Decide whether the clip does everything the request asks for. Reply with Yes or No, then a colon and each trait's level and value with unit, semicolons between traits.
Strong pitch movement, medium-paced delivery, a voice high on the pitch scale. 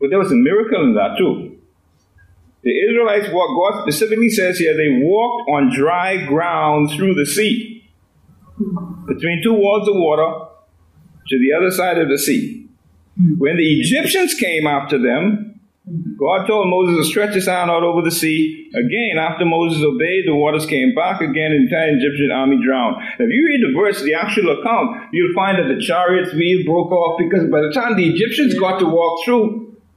No: wide, 6.1 semitones; average, 190 wpm; medium, 180 Hz